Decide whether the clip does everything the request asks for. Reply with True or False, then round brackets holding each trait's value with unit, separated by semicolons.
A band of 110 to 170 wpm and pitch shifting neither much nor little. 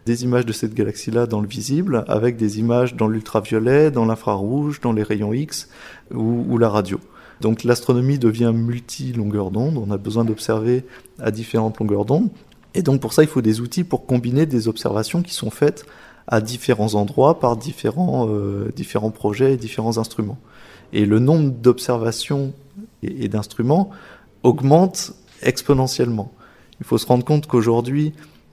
True (160 wpm; 3.7 semitones)